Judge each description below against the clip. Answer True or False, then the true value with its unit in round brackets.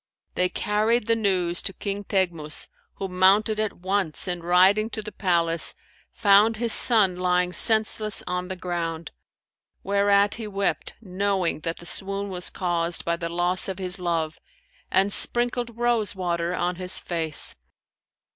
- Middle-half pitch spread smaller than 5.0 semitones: True (2.8 semitones)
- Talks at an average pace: True (150 wpm)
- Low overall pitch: False (190 Hz)